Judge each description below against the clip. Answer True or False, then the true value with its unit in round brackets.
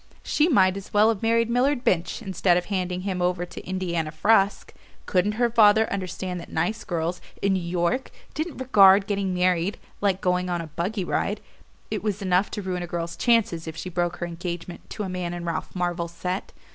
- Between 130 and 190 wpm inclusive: False (200 wpm)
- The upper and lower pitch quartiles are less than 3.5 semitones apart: True (2.9 semitones)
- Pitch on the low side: False (185 Hz)